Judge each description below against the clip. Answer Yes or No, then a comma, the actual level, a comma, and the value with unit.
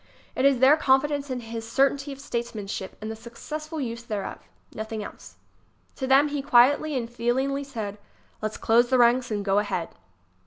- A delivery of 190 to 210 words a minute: No, average, 170 wpm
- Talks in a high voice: Yes, high, 245 Hz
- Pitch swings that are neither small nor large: Yes, average, 3.6 semitones